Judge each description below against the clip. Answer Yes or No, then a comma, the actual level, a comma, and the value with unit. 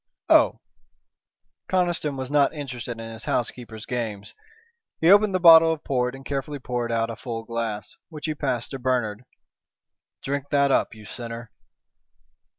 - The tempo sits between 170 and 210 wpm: No, average, 155 wpm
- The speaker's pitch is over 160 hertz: No, low, 125 Hz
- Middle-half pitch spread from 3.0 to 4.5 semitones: Yes, average, 4.0 semitones